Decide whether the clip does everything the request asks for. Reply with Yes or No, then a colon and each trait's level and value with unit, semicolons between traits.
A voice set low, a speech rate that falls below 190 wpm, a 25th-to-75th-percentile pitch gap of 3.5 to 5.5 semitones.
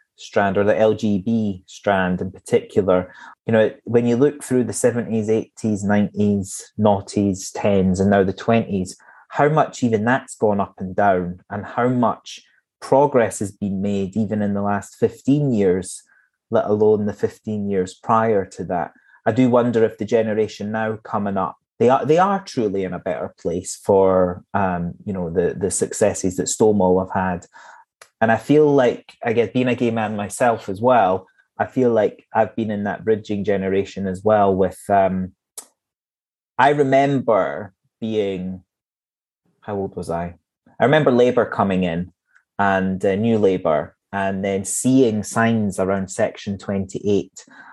No: low, 100 Hz; average, 165 wpm; average, 2.8 semitones